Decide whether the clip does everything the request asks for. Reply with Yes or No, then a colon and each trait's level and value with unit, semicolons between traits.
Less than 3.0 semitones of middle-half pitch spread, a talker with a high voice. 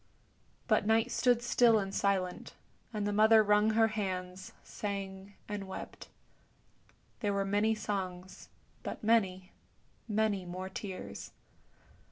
Yes: narrow, 2.4 semitones; high, 205 Hz